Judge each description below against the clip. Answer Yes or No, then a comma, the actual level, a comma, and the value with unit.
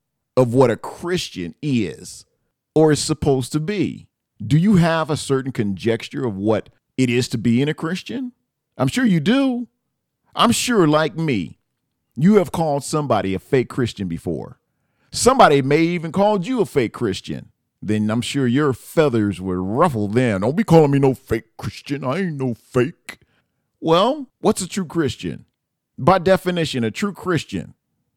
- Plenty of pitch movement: Yes, wide, 6.9 semitones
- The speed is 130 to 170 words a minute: Yes, average, 165 wpm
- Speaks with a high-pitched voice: No, medium, 140 Hz